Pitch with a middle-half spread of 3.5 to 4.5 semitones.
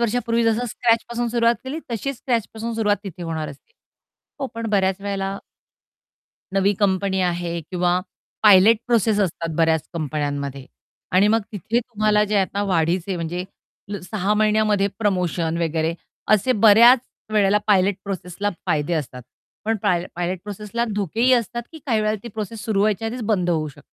Yes: average, 4.1 semitones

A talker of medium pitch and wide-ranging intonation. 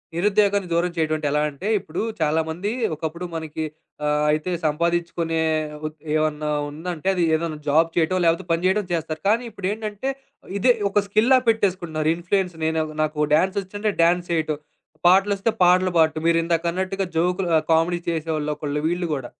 No: medium, 170 Hz; average, 3.2 semitones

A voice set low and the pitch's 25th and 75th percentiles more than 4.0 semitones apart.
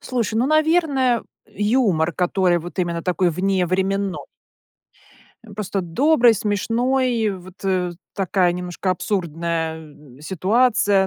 No: high, 190 Hz; average, 4.5 semitones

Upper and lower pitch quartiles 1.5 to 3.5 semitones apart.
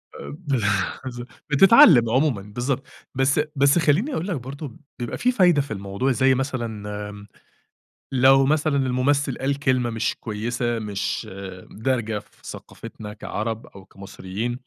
No: average, 4.1 semitones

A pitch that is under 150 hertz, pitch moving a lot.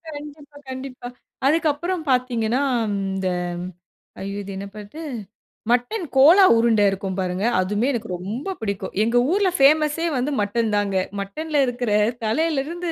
No: high, 245 Hz; wide, 6.7 semitones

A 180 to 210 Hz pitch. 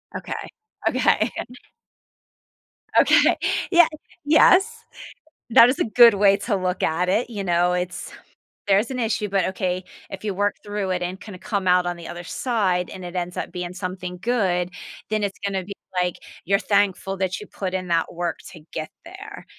Yes: high, 190 Hz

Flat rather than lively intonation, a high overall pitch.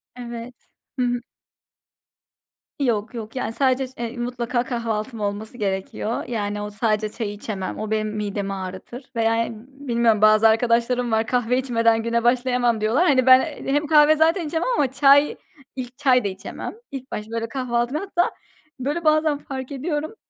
No: average, 3.3 semitones; high, 240 Hz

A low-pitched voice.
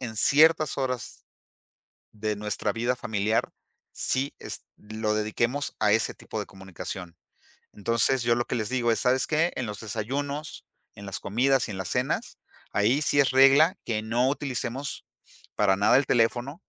Yes: low, 120 Hz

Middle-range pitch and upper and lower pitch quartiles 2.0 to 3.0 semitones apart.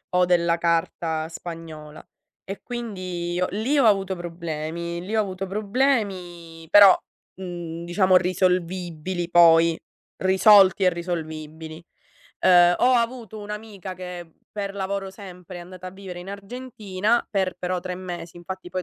Yes: medium, 180 Hz; narrow, 2.5 semitones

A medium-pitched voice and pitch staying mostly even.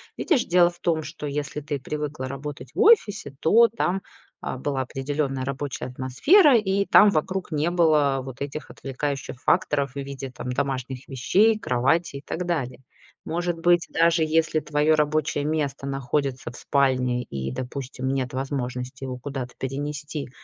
No: medium, 145 Hz; average, 3.7 semitones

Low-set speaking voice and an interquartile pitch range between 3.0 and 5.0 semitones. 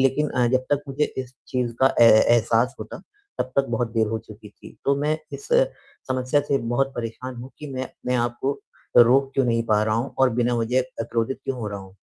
No: low, 125 Hz; narrow, 2.6 semitones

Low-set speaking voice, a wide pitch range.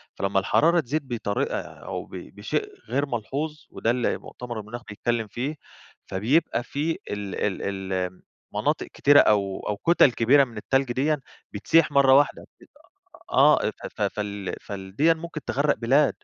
Yes: low, 120 Hz; wide, 5.9 semitones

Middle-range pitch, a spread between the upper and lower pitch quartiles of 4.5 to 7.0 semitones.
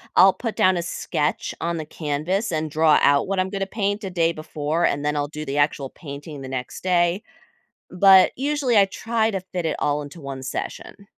Yes: medium, 170 Hz; average, 4.8 semitones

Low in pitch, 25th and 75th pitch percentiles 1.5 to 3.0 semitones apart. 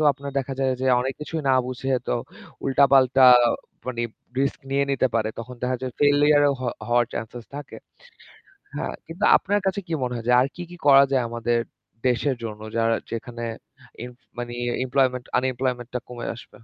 Yes: low, 130 Hz; narrow, 2.4 semitones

